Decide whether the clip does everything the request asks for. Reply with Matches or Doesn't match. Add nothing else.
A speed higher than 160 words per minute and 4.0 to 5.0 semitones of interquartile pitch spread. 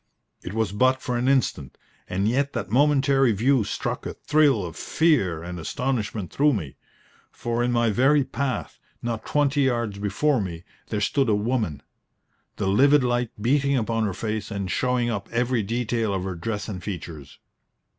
Matches